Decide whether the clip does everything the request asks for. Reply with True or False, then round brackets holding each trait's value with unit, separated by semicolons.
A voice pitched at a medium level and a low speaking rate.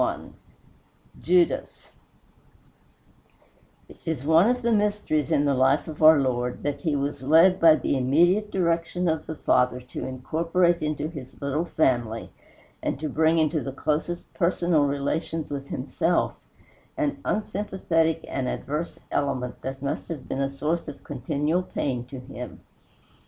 False (155 Hz; 145 wpm)